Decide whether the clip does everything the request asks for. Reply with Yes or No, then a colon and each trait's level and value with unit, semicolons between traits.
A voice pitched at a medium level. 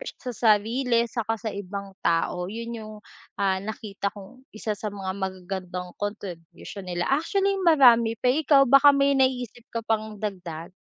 No: high, 215 Hz